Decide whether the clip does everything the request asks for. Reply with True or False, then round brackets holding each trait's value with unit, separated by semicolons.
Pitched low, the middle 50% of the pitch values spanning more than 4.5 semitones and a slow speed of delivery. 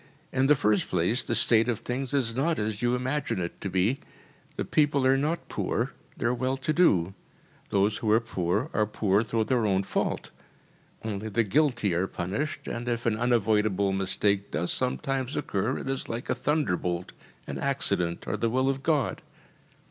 False (115 Hz; 5.1 semitones; 185 wpm)